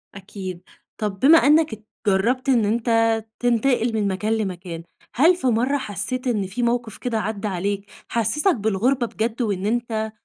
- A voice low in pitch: No, high, 225 Hz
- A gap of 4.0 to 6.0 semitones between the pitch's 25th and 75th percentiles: No, average, 3.4 semitones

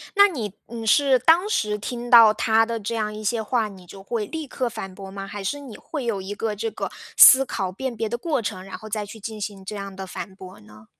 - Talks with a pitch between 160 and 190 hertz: No, high, 215 Hz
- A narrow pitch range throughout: No, average, 3.4 semitones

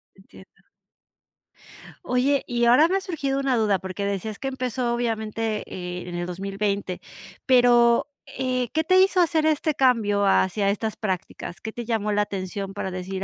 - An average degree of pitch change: Yes, average, 4.6 semitones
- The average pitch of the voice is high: Yes, high, 220 Hz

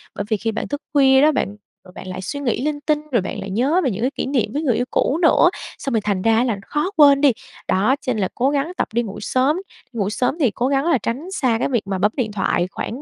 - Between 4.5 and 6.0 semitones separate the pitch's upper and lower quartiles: Yes, average, 5.2 semitones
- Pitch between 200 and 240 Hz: No, very high, 250 Hz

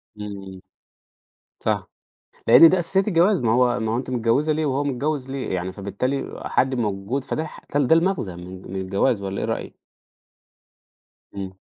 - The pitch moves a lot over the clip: Yes, wide, 6.8 semitones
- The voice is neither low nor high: No, low, 125 Hz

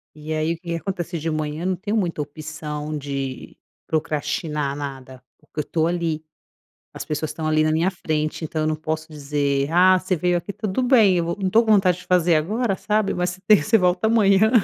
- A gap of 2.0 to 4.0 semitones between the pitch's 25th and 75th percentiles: Yes, average, 3.5 semitones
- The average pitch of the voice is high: No, medium, 165 Hz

